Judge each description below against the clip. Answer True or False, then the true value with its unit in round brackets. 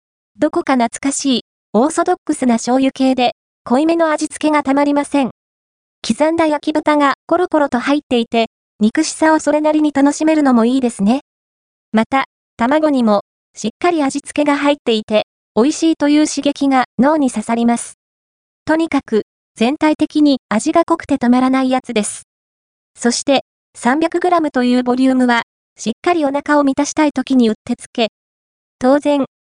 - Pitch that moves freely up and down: False (4.1 semitones)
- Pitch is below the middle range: False (275 Hz)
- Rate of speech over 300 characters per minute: True (330 characters per minute)